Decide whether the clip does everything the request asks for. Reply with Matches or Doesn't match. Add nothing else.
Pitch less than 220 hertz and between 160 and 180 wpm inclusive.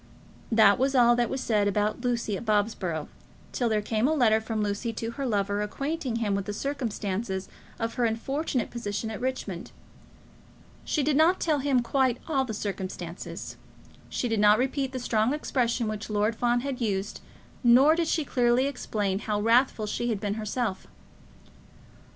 Doesn't match